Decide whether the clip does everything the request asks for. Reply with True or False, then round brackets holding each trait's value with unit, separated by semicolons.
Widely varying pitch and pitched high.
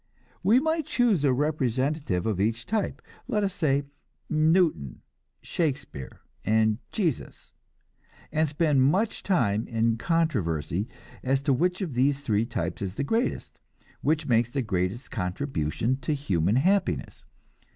False (6.8 semitones; 135 Hz)